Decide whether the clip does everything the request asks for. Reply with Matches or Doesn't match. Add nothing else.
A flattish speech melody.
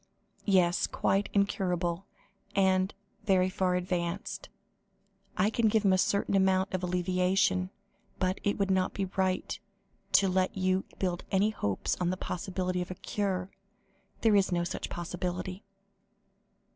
Matches